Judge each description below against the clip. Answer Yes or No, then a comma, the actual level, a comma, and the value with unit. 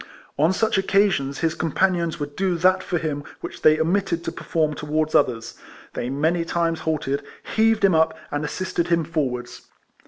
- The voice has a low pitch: No, medium, 160 Hz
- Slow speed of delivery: No, average, 165 wpm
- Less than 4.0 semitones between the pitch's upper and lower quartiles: Yes, average, 3.5 semitones